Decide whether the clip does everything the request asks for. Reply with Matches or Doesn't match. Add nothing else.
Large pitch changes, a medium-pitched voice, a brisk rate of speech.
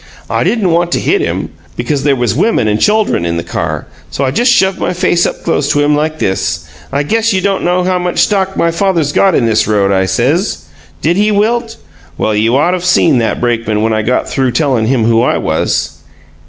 Matches